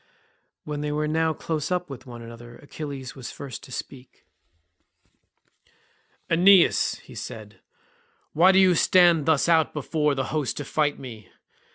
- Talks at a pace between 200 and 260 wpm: No, average, 150 wpm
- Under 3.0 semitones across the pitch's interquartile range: No, average, 3.7 semitones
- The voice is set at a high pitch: No, medium, 150 Hz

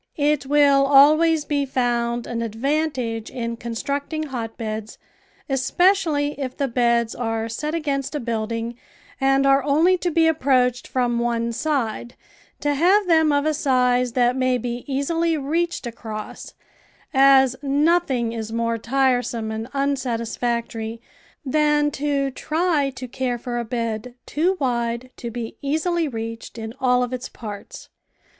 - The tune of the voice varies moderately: Yes, average, 3.8 semitones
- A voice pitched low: No, very high, 255 Hz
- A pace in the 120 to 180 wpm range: Yes, average, 140 wpm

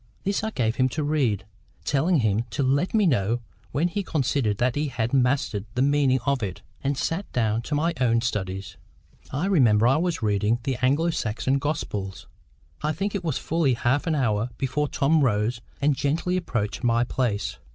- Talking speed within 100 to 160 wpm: No, average, 190 wpm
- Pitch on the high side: No, low, 130 Hz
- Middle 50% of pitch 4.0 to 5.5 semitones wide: Yes, average, 4.8 semitones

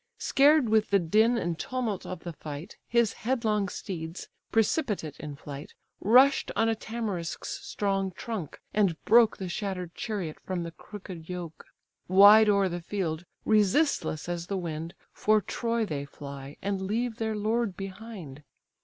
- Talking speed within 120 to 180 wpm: Yes, average, 150 wpm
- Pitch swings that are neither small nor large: Yes, average, 4.7 semitones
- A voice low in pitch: No, high, 195 Hz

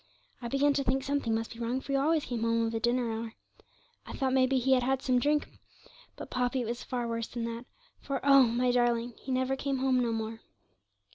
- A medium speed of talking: No, fast, 225 wpm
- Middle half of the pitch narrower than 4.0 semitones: Yes, narrow, 2.5 semitones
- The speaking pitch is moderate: No, very high, 250 Hz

